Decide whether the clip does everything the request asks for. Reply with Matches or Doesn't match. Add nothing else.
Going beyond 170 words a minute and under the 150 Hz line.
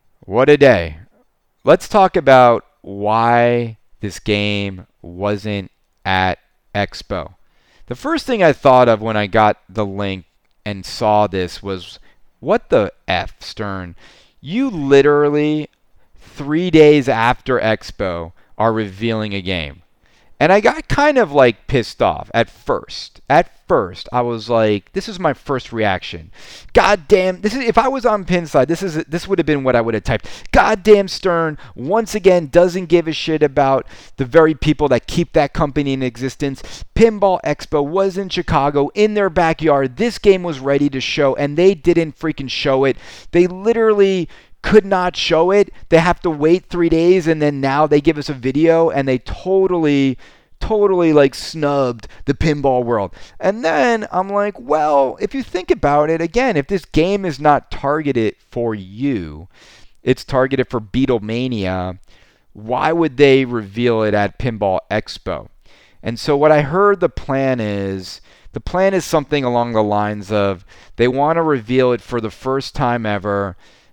Doesn't match